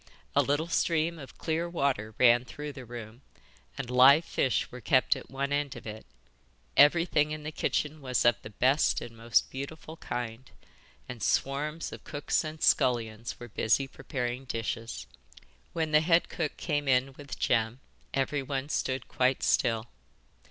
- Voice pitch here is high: No, low, 135 Hz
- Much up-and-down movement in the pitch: No, average, 3.7 semitones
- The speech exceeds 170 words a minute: No, average, 160 wpm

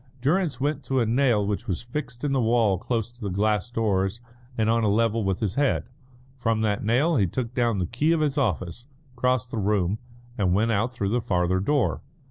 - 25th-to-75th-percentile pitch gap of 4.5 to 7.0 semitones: No, average, 3.9 semitones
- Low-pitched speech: Yes, low, 115 Hz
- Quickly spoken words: Yes, fast, 215 wpm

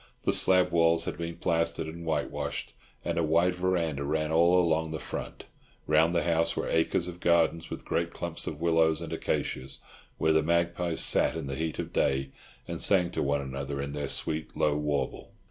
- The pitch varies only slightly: Yes, narrow, 1.8 semitones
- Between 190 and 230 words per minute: Yes, average, 195 wpm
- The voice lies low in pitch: Yes, very low, 80 Hz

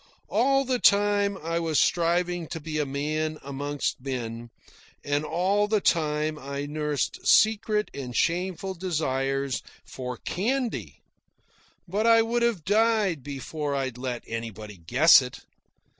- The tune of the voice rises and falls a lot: Yes, wide, 6.6 semitones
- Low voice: No, medium, 155 Hz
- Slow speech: Yes, slow, 130 wpm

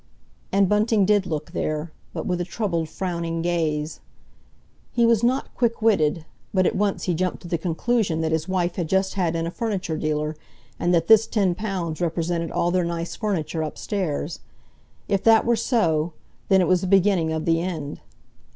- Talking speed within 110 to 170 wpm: No, average, 185 wpm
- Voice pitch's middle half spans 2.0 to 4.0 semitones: Yes, average, 3.5 semitones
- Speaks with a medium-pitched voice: Yes, medium, 175 Hz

